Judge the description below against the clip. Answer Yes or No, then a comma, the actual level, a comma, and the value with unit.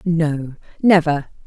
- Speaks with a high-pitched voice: No, medium, 160 Hz